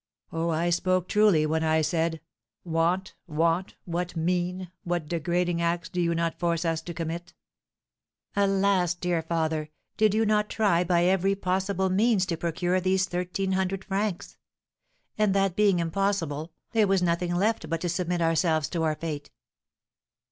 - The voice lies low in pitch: No, medium, 175 Hz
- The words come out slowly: No, average, 155 wpm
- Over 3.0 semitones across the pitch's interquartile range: No, narrow, 2.4 semitones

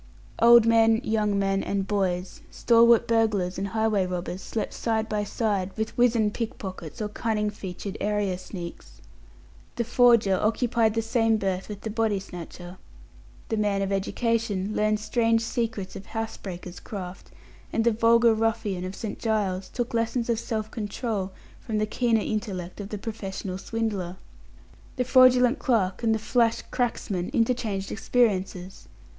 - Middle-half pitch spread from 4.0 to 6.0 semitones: No, average, 2.9 semitones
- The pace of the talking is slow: No, average, 150 wpm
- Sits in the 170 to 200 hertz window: No, high, 215 Hz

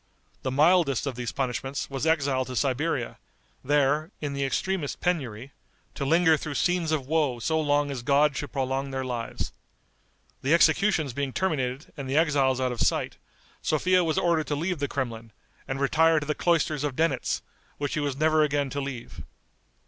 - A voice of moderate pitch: Yes, medium, 145 Hz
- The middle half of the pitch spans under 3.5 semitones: Yes, average, 3.0 semitones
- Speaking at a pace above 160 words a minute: Yes, average, 180 wpm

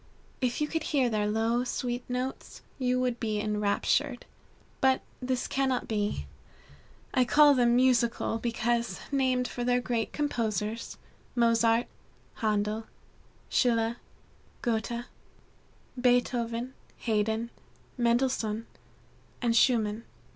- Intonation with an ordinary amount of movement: No, narrow, 2.0 semitones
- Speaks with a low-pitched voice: No, high, 235 Hz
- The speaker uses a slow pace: Yes, slow, 105 wpm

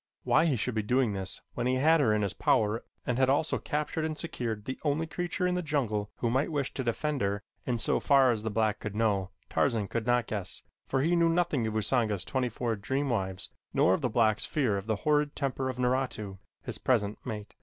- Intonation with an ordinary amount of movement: Yes, average, 5.0 semitones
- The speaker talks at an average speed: No, fast, 230 wpm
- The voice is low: Yes, low, 125 Hz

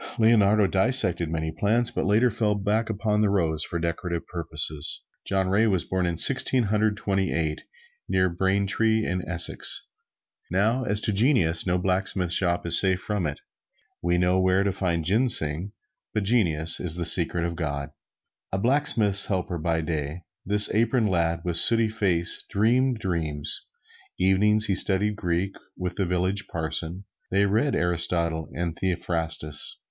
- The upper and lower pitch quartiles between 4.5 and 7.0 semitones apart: No, average, 3.8 semitones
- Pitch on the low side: Yes, very low, 95 Hz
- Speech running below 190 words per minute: Yes, average, 155 wpm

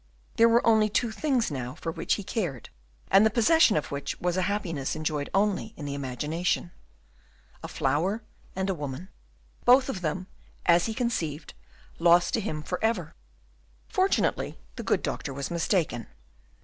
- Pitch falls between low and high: Yes, medium, 180 Hz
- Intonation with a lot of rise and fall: Yes, wide, 6.5 semitones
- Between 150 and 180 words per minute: Yes, average, 160 wpm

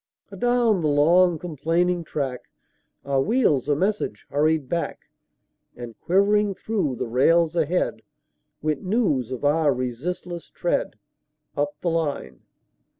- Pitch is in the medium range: Yes, medium, 160 Hz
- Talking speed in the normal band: No, slow, 120 wpm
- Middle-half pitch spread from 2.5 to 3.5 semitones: No, average, 4.4 semitones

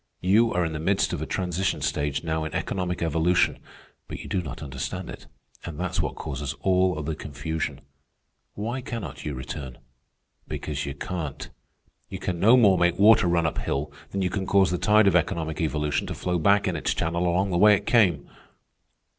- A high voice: No, very low, 85 Hz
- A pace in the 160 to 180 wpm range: No, average, 195 wpm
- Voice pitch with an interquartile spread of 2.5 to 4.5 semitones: Yes, average, 3.7 semitones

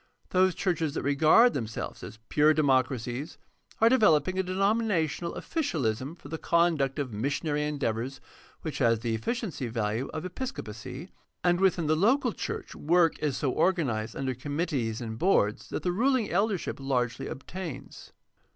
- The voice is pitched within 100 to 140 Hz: No, medium, 150 Hz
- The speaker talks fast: No, average, 150 wpm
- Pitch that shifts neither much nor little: No, wide, 6.3 semitones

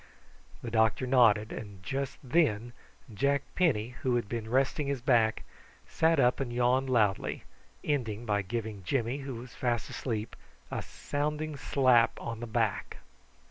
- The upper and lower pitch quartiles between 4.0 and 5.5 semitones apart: No, average, 3.5 semitones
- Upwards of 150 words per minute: No, average, 145 wpm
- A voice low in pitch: Yes, low, 120 Hz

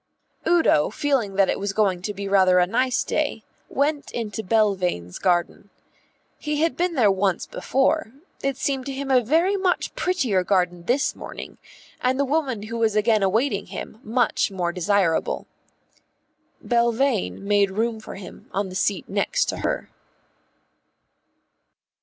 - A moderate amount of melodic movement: No, wide, 5.7 semitones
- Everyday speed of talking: Yes, average, 150 wpm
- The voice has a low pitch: No, high, 220 Hz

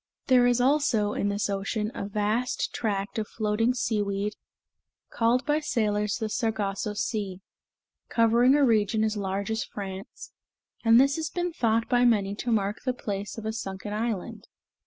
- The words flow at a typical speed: Yes, average, 160 wpm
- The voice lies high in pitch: Yes, high, 220 Hz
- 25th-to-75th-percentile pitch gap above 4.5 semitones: No, average, 2.9 semitones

